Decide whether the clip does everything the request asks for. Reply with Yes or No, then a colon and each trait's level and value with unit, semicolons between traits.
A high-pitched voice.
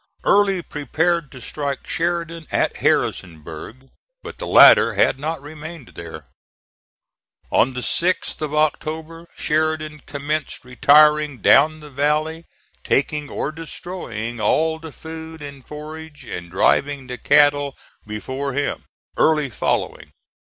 No: medium, 150 Hz